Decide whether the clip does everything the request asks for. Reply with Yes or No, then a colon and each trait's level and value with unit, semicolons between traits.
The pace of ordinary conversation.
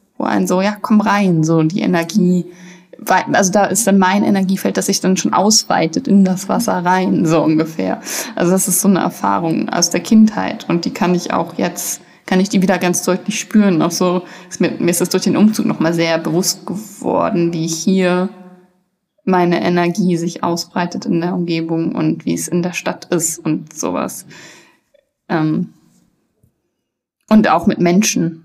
Yes: average, 175 wpm